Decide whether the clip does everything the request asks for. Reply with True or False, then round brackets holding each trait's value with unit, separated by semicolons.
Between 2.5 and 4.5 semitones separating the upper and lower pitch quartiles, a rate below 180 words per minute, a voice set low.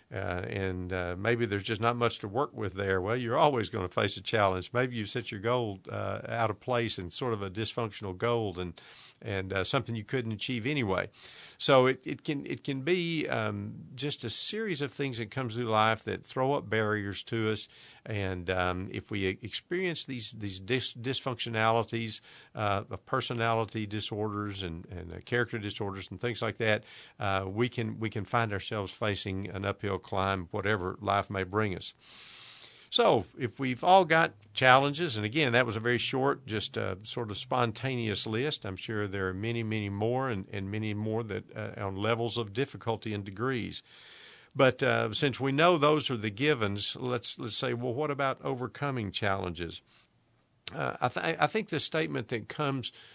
False (3.9 semitones; 190 wpm; 110 Hz)